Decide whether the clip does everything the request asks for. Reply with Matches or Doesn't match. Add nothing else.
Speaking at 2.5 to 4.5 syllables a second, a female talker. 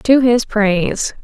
Matches